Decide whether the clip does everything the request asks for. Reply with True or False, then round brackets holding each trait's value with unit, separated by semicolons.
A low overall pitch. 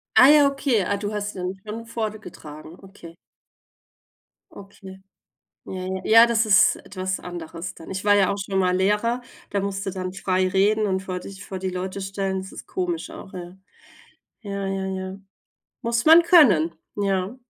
False (195 Hz)